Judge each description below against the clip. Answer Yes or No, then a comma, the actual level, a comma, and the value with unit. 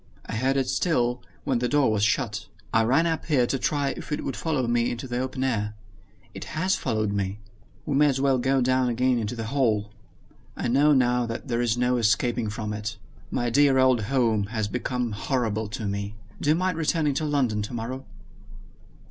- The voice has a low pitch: Yes, low, 125 Hz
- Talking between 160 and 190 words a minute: No, average, 200 wpm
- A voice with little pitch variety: No, average, 3.4 semitones